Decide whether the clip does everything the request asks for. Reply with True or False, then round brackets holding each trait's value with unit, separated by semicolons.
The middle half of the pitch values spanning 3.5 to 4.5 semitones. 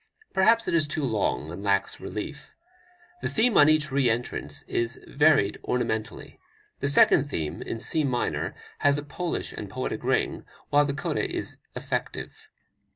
False (5.5 semitones)